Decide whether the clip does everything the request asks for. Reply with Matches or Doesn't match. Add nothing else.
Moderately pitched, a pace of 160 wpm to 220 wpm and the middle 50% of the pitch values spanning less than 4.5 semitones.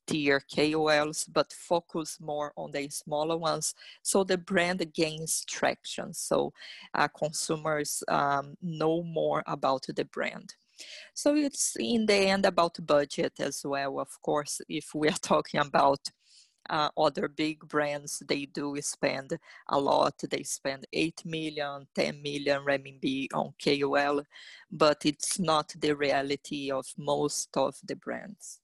Doesn't match